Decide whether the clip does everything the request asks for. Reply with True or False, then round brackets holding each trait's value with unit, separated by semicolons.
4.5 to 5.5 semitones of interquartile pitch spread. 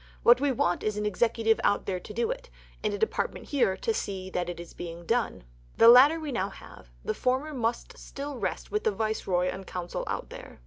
True (5.2 semitones)